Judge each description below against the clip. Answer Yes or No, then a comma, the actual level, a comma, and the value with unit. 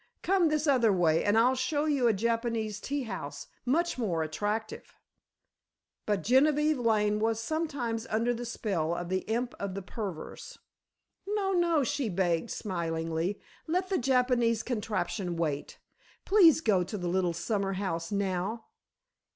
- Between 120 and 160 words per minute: Yes, average, 145 wpm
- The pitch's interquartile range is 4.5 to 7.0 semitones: Yes, wide, 5.6 semitones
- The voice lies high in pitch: Yes, high, 225 Hz